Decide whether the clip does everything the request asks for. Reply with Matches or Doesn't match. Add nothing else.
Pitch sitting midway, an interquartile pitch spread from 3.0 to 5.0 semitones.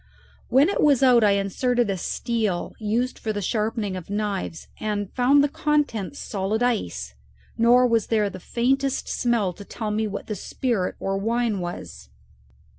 Doesn't match